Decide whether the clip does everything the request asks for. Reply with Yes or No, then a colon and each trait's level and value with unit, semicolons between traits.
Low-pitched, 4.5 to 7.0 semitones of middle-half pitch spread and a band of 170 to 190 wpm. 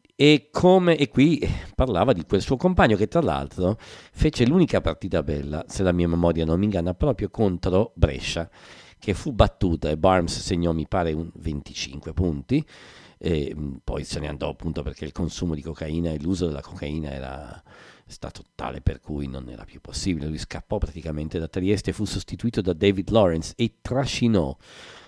Yes: very low, 85 Hz; average, 5.1 semitones; average, 180 wpm